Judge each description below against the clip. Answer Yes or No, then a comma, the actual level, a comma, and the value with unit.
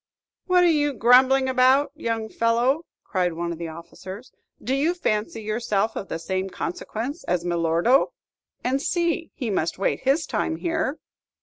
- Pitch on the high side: Yes, high, 235 Hz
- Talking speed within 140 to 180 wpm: Yes, average, 160 wpm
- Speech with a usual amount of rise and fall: No, wide, 7.0 semitones